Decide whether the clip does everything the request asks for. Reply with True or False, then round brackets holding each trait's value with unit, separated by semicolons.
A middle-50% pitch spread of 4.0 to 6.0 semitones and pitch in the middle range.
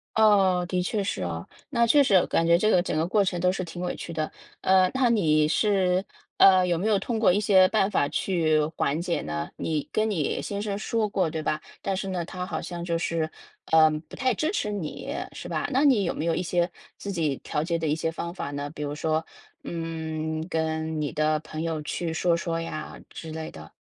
False (3.6 semitones; 170 Hz)